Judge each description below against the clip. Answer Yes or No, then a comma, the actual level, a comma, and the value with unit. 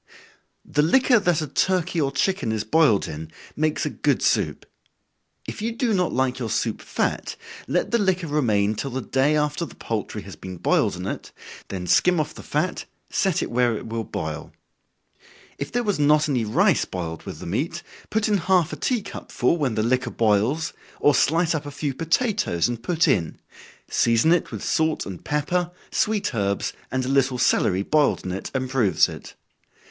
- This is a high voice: No, medium, 145 Hz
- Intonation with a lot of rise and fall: Yes, wide, 7.4 semitones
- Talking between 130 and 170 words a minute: No, average, 195 wpm